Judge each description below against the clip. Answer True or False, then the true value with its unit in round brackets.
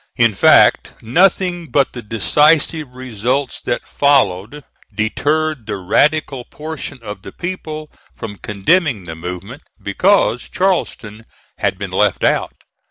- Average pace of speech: False (120 wpm)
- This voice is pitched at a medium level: False (130 Hz)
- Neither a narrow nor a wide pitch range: False (6.6 semitones)